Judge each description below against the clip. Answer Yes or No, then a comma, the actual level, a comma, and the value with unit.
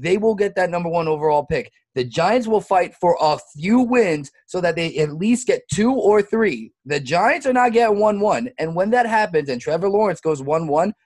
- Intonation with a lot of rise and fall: Yes, wide, 5.7 semitones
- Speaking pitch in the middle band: Yes, medium, 180 Hz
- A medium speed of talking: No, fast, 230 wpm